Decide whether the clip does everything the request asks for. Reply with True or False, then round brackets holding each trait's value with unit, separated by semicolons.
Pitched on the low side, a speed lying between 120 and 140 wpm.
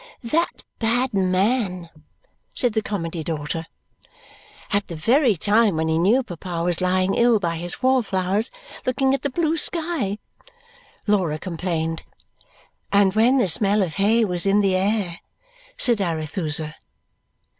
False (195 Hz; 135 wpm)